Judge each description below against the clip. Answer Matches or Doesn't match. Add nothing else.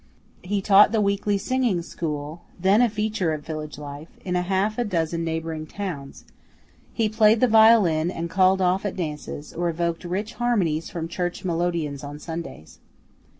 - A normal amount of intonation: Matches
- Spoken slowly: Doesn't match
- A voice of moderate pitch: Matches